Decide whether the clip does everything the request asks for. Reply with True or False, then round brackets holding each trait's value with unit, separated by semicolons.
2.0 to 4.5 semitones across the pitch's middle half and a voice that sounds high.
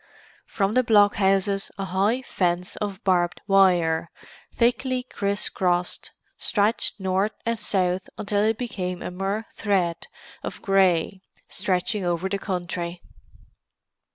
True (2.5 semitones; 195 Hz)